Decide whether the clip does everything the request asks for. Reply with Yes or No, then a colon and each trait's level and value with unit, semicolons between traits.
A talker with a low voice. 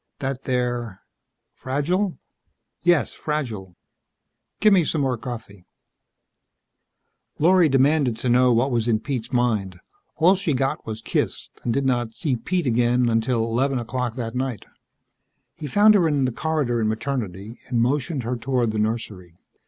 Yes: low, 125 Hz